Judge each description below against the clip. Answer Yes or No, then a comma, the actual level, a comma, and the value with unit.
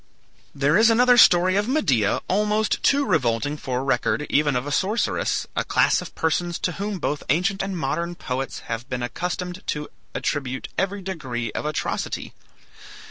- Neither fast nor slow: Yes, average, 160 wpm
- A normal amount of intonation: No, wide, 6.2 semitones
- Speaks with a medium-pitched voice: Yes, medium, 165 Hz